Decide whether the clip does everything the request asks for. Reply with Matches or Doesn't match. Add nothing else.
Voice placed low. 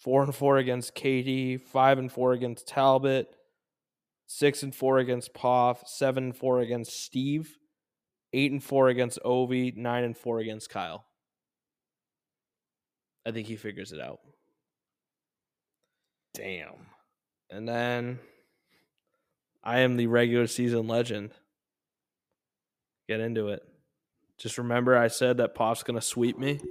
Matches